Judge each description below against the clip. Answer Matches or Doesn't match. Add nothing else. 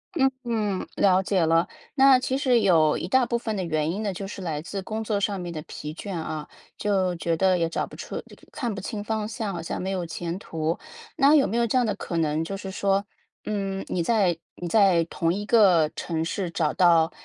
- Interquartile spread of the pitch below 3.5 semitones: Doesn't match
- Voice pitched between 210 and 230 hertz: Doesn't match